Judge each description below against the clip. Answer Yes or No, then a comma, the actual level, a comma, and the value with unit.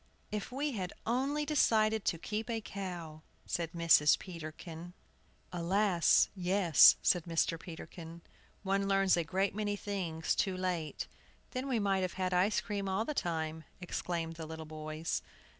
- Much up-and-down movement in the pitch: No, average, 3.7 semitones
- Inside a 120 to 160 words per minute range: Yes, average, 150 wpm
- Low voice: No, medium, 185 Hz